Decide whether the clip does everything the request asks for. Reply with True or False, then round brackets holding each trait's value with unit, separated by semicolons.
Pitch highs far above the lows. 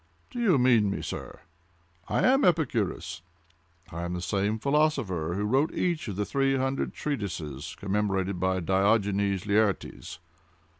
True (6.7 semitones)